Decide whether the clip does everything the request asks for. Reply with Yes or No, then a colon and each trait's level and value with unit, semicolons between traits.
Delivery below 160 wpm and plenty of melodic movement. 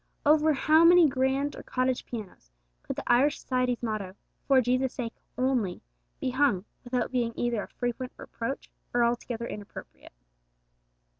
No: average, 145 wpm; narrow, 2.4 semitones